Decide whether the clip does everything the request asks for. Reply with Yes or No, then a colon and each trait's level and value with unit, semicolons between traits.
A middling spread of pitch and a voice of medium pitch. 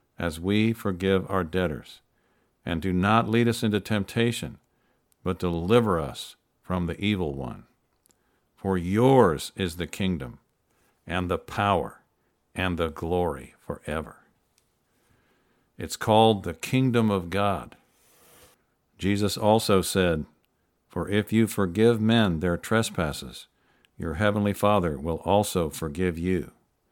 No: average, 3.7 semitones; very low, 95 Hz